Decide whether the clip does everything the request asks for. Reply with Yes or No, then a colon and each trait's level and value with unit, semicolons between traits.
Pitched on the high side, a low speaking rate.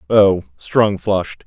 No: very low, 95 Hz; slow, 125 wpm